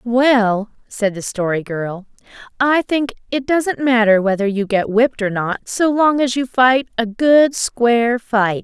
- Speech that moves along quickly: No, average, 175 wpm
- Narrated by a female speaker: Yes, female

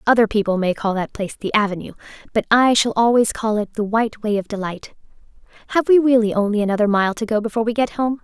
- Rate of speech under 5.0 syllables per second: No, 6.6 syllables/s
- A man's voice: No, female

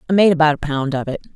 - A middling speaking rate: No, fast, 310 wpm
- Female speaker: Yes, female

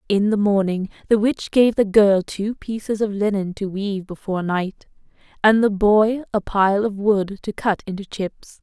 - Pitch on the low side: No, high, 205 Hz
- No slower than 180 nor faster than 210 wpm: Yes, average, 190 wpm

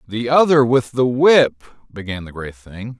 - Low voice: Yes, low, 115 Hz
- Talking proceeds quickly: No, average, 180 wpm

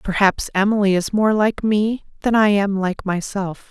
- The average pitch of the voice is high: Yes, high, 200 Hz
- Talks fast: No, average, 180 wpm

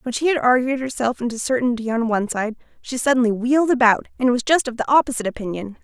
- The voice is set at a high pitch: Yes, high, 245 Hz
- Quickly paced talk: Yes, fast, 215 wpm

